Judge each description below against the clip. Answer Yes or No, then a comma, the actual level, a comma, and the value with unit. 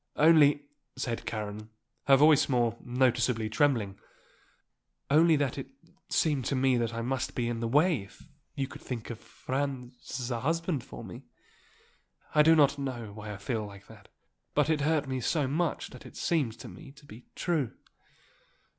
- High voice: No, low, 130 Hz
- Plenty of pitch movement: No, average, 4.1 semitones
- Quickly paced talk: No, average, 175 wpm